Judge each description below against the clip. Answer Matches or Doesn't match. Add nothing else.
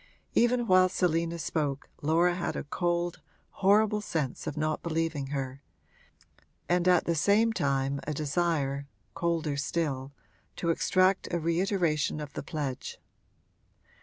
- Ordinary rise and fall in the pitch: Matches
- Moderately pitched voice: Matches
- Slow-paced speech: Matches